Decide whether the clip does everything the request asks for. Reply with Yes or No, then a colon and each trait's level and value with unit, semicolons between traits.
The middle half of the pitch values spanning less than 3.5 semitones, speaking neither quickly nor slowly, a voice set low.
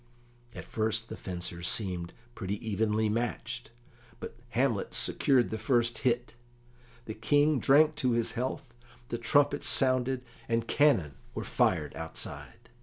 No: average, 3.1 semitones; slow, 130 wpm; low, 115 Hz